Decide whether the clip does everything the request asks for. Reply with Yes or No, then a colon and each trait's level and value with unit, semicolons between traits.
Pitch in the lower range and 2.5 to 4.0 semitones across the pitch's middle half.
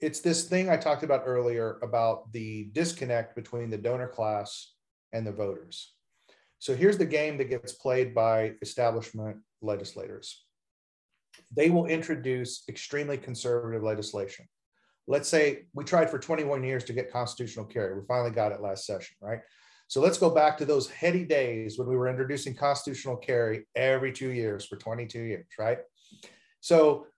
No: low, 125 Hz; average, 4.6 semitones